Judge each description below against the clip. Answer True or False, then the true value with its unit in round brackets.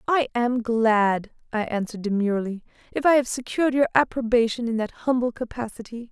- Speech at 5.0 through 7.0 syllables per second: True (5.7 syllables/s)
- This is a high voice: True (235 Hz)